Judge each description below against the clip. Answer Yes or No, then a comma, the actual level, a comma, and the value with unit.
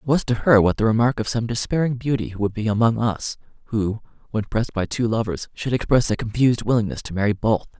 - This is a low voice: Yes, low, 115 Hz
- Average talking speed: No, fast, 225 wpm